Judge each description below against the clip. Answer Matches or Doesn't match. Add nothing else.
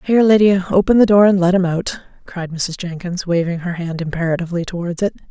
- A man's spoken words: Doesn't match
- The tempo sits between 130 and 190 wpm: Doesn't match